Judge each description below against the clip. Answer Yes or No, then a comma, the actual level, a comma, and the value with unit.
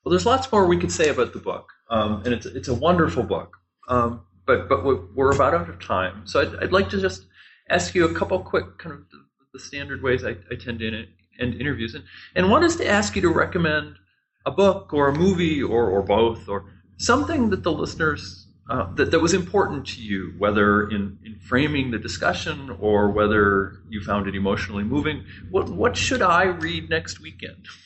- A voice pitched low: Yes, low, 115 Hz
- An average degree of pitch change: No, wide, 6.1 semitones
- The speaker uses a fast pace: Yes, fast, 215 wpm